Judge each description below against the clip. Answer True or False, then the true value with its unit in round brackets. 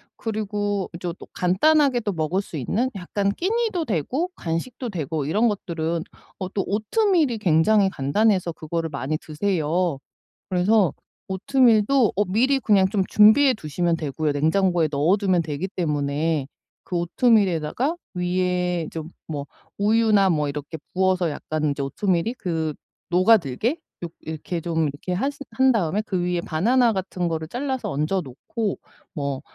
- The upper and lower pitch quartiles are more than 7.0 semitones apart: False (5.2 semitones)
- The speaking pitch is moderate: True (180 Hz)